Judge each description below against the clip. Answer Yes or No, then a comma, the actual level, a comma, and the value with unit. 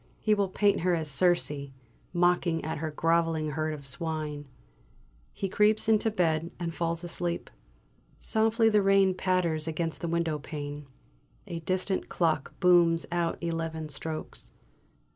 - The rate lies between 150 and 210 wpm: No, average, 140 wpm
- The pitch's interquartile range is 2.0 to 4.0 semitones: Yes, average, 2.7 semitones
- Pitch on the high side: No, medium, 170 Hz